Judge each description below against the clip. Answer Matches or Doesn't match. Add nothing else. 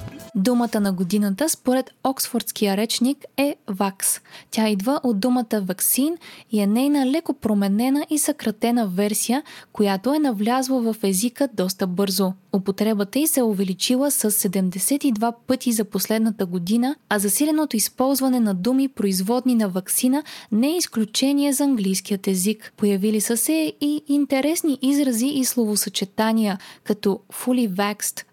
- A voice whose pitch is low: Doesn't match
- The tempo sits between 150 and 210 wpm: Doesn't match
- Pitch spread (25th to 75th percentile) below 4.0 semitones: Doesn't match